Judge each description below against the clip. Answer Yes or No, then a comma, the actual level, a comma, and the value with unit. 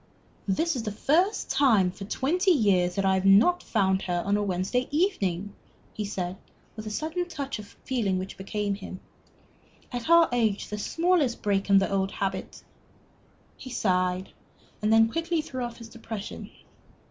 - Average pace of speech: Yes, average, 170 wpm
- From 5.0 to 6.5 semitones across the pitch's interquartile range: Yes, wide, 5.6 semitones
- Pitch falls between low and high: No, high, 210 Hz